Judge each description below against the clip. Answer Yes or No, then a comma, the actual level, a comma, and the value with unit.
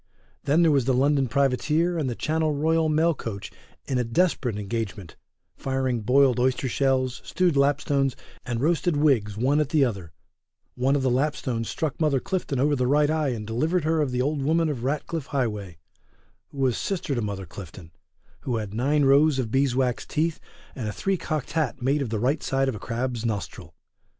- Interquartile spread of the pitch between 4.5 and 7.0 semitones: No, average, 4.0 semitones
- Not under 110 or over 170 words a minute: No, average, 195 wpm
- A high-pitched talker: No, low, 135 Hz